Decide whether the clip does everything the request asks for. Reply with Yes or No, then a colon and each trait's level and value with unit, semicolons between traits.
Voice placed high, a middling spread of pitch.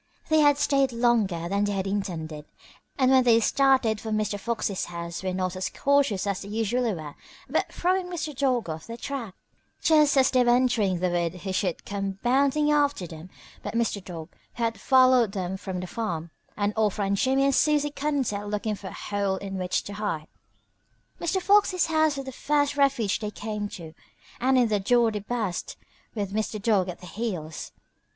No: high, 215 Hz; wide, 5.7 semitones